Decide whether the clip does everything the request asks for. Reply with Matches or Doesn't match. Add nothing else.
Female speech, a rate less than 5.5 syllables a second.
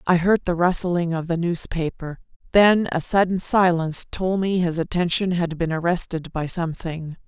Matches